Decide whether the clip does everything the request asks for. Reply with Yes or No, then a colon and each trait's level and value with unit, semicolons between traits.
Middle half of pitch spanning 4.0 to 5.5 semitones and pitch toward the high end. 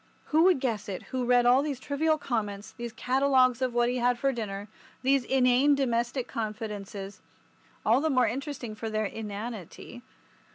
No: average, 3.6 semitones; high, 245 Hz